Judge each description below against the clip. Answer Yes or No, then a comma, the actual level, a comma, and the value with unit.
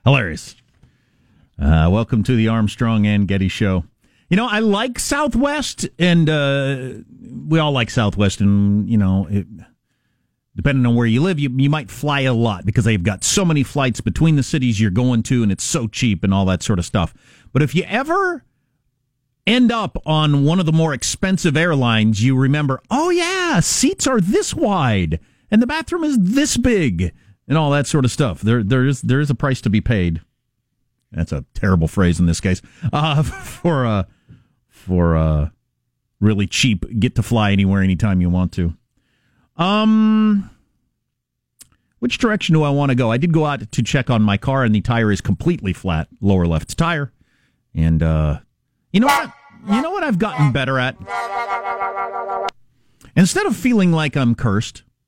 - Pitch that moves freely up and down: Yes, wide, 7.7 semitones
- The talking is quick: No, average, 180 wpm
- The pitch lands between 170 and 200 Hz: No, low, 125 Hz